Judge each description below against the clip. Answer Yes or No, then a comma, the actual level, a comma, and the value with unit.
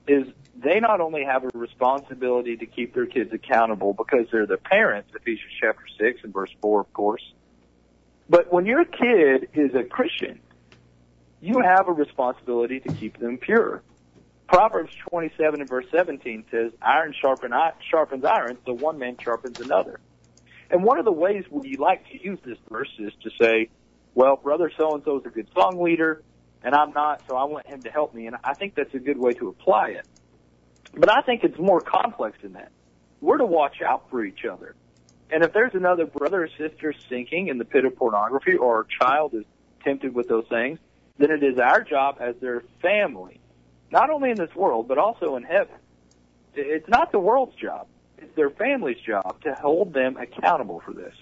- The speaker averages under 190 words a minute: No, average, 195 wpm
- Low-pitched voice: Yes, low, 130 Hz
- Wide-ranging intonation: Yes, wide, 7.8 semitones